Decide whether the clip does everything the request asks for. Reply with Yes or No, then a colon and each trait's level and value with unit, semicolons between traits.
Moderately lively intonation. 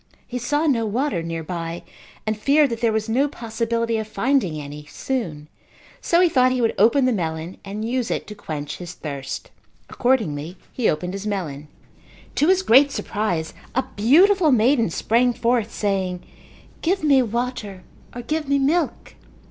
No: wide, 6.4 semitones